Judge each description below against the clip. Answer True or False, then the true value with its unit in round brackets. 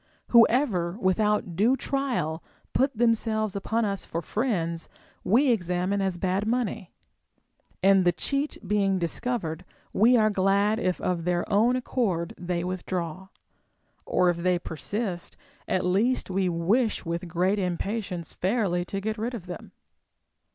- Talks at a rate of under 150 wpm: True (140 wpm)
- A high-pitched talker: True (195 Hz)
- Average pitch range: True (4.0 semitones)